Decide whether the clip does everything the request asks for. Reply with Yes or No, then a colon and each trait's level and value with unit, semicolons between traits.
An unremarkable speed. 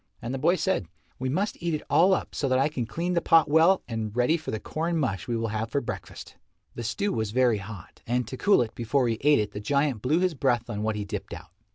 No: fast, 265 wpm